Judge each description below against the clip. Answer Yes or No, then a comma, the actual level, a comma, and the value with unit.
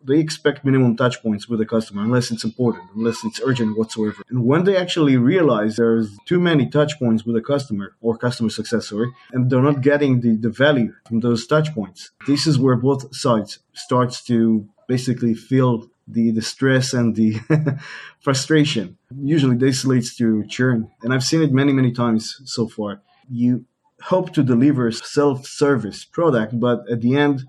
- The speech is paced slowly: No, average, 180 wpm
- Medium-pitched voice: No, low, 125 Hz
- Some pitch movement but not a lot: Yes, average, 3.5 semitones